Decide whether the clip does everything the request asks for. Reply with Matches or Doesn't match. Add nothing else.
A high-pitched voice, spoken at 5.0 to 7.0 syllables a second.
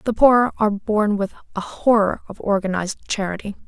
Matches